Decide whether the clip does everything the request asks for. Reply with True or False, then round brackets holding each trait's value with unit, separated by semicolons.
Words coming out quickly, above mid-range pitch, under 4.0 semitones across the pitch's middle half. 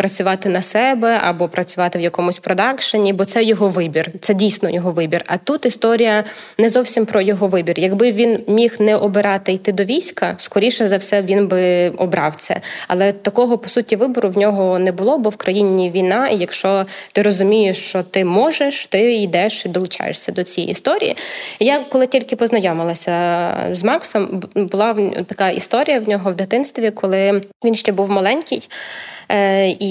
True (170 wpm; 200 Hz; 3.1 semitones)